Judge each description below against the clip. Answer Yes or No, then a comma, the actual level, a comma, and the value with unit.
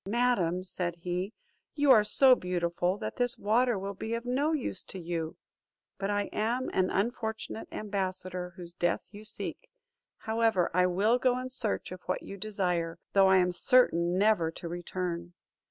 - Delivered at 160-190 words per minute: Yes, average, 170 wpm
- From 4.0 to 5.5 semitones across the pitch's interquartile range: Yes, average, 4.4 semitones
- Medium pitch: No, high, 195 Hz